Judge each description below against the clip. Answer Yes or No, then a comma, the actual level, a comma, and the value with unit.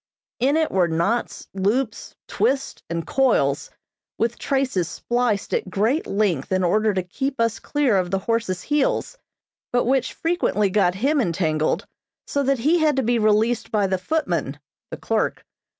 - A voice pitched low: No, high, 220 Hz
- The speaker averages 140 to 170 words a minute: Yes, average, 160 wpm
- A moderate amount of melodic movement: No, wide, 6.3 semitones